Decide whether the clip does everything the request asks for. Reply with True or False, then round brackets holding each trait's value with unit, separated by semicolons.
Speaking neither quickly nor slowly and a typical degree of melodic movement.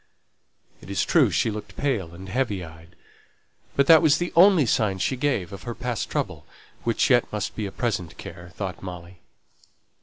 False (180 wpm; 6.3 semitones)